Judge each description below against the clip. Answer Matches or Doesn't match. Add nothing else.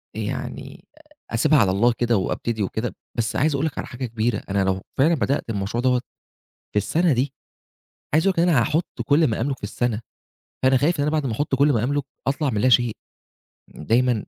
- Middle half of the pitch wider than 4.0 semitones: Matches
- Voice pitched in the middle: Doesn't match